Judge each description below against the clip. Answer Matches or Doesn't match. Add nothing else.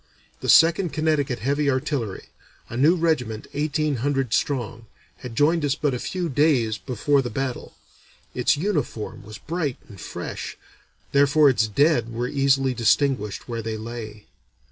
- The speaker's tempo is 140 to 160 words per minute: Matches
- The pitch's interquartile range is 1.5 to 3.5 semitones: Doesn't match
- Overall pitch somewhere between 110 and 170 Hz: Matches